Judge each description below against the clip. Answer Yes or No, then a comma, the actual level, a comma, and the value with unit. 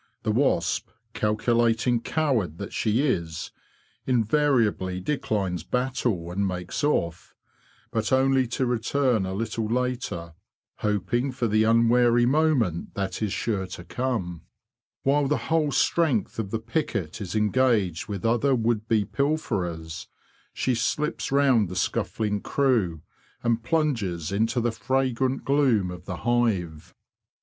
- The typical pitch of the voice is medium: No, low, 115 Hz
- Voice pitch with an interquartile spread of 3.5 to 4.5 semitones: No, average, 5.1 semitones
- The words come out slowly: Yes, slow, 130 wpm